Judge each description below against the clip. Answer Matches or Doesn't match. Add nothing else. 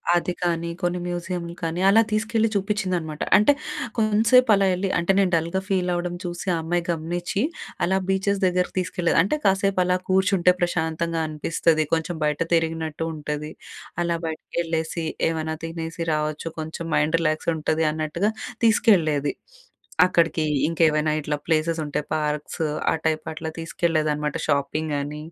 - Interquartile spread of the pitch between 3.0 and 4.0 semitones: Doesn't match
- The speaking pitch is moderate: Matches